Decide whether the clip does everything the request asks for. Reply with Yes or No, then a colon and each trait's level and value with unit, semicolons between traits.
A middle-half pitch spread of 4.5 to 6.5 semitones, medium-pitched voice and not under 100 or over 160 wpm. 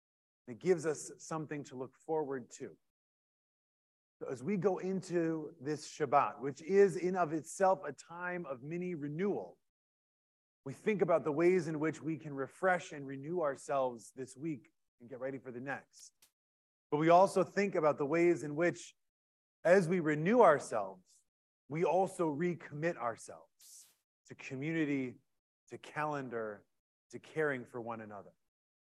Yes: average, 4.8 semitones; medium, 150 Hz; average, 145 wpm